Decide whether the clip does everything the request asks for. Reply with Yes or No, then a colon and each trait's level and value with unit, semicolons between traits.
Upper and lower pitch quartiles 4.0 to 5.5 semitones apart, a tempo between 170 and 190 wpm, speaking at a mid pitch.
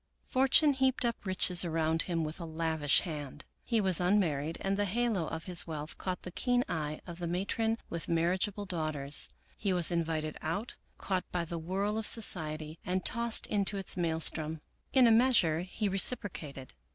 Yes: average, 4.3 semitones; average, 175 wpm; medium, 180 Hz